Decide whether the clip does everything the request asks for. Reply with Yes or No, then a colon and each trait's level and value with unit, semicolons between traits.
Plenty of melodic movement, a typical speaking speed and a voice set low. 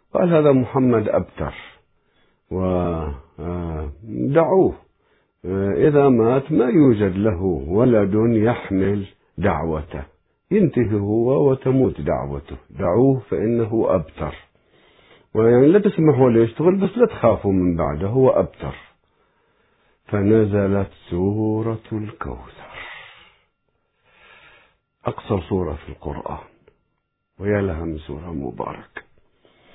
Yes: wide, 6.2 semitones; average, 85 wpm; low, 100 Hz